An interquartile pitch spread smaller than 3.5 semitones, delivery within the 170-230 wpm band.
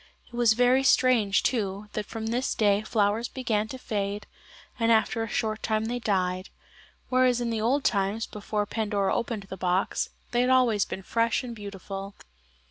Yes: average, 2.9 semitones; average, 175 wpm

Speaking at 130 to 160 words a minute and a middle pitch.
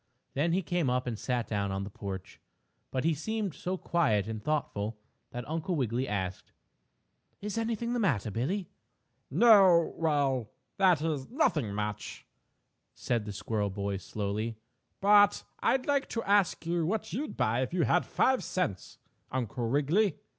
Yes: average, 155 wpm; medium, 145 Hz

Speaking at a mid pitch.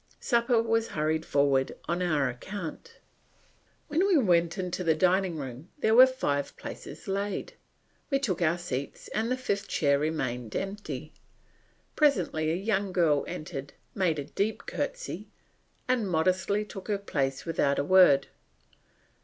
Yes: medium, 180 Hz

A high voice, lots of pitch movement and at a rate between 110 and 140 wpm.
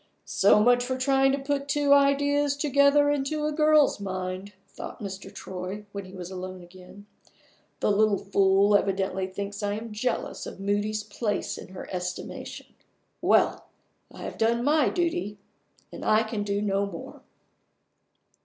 No: high, 210 Hz; wide, 6.2 semitones; average, 155 wpm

